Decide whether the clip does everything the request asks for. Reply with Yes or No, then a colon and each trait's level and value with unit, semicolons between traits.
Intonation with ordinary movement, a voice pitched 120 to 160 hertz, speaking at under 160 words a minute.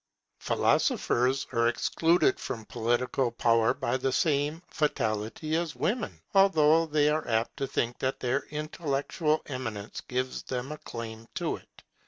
Yes: average, 4.5 semitones; low, 135 Hz; average, 140 wpm